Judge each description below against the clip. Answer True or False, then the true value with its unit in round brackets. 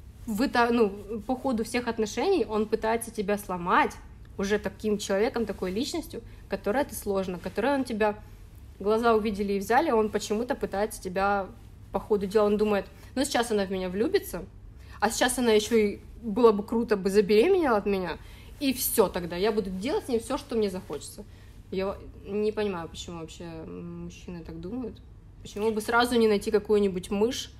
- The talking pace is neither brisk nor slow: False (170 wpm)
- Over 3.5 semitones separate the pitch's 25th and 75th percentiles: False (2.7 semitones)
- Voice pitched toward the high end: True (210 Hz)